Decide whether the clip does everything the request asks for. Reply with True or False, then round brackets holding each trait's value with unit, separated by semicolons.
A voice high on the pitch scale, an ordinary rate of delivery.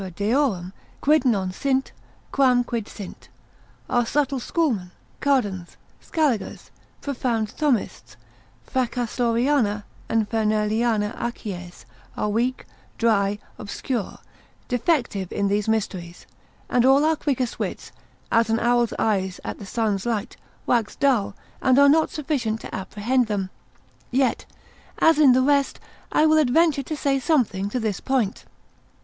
False (235 Hz; 130 wpm)